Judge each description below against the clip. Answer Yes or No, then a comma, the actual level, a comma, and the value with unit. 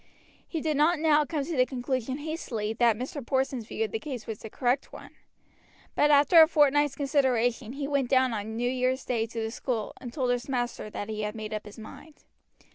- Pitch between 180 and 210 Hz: No, very high, 255 Hz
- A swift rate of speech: Yes, fast, 215 wpm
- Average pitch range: Yes, average, 4.2 semitones